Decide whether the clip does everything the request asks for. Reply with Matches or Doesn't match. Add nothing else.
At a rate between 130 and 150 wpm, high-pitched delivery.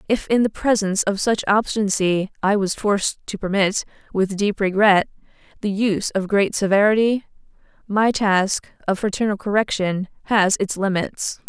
Matches